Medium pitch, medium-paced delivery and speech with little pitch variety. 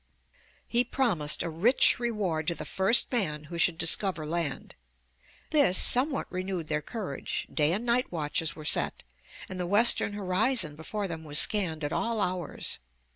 No: medium, 180 Hz; average, 160 wpm; wide, 5.6 semitones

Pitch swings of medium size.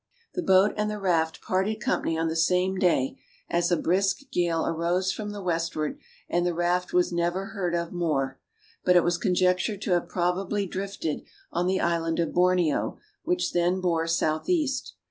No: narrow, 2.1 semitones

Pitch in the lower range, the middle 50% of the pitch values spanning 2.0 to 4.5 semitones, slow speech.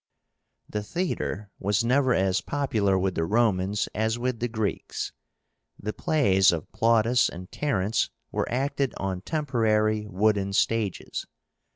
Yes: low, 110 Hz; average, 3.8 semitones; slow, 130 wpm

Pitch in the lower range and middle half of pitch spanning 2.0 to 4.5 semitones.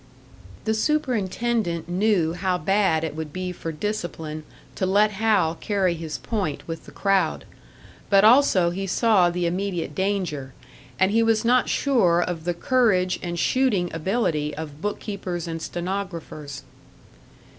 No: medium, 185 Hz; average, 4.2 semitones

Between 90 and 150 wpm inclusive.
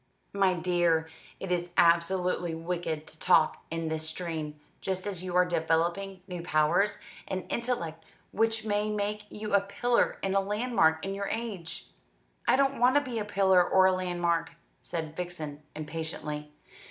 No: average, 160 wpm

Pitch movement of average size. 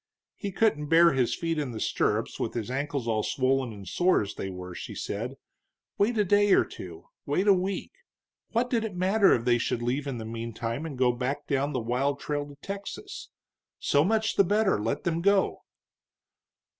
No: wide, 8.1 semitones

